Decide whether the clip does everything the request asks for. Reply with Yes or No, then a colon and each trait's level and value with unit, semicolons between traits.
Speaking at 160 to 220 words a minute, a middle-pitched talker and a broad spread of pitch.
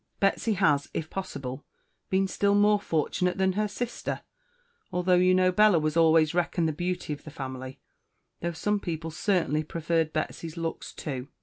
No: average, 165 wpm; medium, 170 Hz; average, 3.5 semitones